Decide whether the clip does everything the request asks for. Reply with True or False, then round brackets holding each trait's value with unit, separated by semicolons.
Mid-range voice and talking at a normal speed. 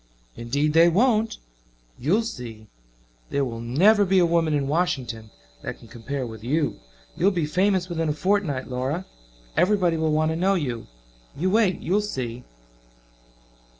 True (160 Hz; 150 wpm)